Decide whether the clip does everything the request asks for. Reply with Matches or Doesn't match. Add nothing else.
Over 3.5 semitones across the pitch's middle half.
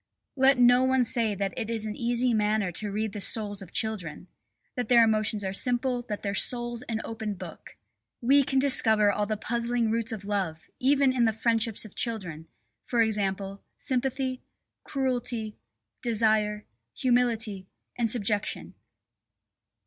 Doesn't match